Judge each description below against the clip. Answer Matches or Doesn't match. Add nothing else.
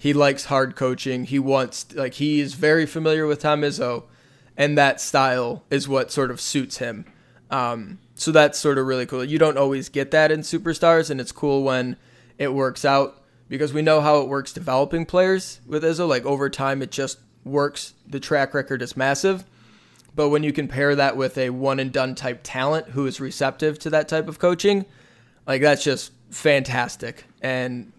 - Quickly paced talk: Doesn't match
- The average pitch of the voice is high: Doesn't match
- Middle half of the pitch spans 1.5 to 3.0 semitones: Matches